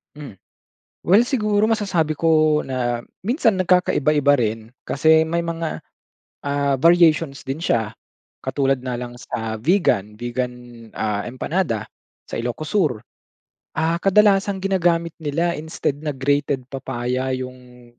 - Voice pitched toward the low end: No, medium, 145 Hz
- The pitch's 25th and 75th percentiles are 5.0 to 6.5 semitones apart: Yes, wide, 5.4 semitones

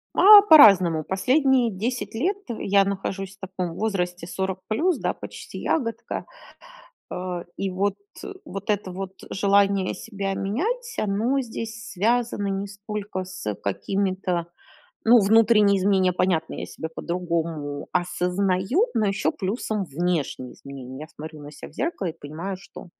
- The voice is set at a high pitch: Yes, high, 195 Hz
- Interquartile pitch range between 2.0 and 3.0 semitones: No, average, 3.7 semitones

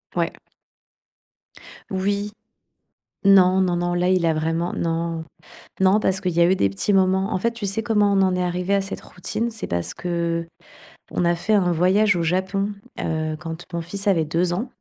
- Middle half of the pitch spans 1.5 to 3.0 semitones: Yes, average, 2.7 semitones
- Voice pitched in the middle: Yes, medium, 180 Hz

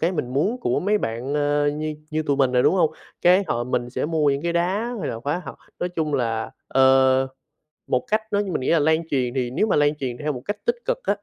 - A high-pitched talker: No, medium, 145 Hz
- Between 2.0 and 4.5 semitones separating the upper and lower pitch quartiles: No, average, 5.2 semitones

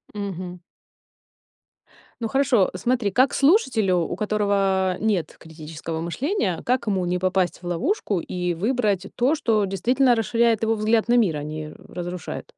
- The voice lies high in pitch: Yes, high, 200 Hz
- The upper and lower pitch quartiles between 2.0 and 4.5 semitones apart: No, average, 4.9 semitones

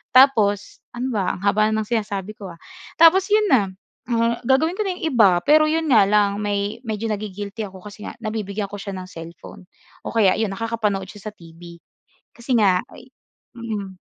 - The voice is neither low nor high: No, high, 210 Hz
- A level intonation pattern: No, average, 3.1 semitones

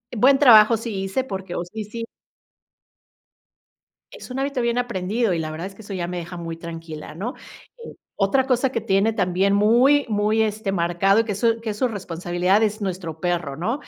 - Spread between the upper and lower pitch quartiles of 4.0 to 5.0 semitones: Yes, average, 4.5 semitones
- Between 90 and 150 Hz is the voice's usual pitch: No, high, 205 Hz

